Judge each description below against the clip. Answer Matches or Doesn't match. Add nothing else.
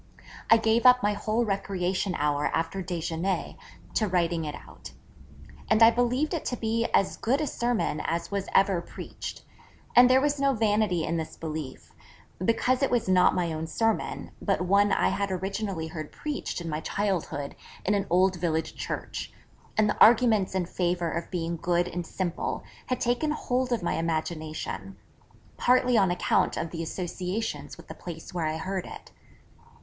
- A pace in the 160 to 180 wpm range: Matches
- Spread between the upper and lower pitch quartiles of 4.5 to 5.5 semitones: Matches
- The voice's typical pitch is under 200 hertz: Matches